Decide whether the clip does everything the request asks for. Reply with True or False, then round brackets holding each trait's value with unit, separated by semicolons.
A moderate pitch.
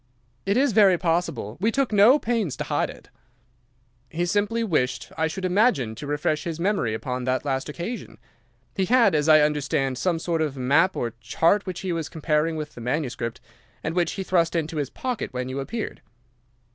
True (165 Hz)